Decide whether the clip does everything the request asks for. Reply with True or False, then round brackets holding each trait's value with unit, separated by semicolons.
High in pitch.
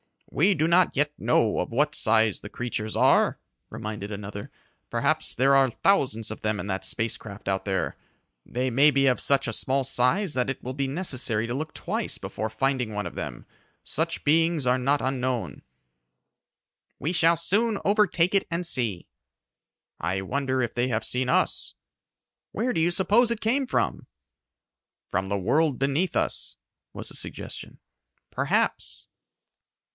False (130 Hz)